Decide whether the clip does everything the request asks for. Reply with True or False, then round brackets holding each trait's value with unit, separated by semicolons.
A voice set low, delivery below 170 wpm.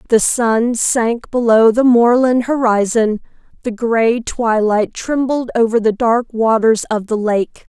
False (230 Hz; 140 wpm)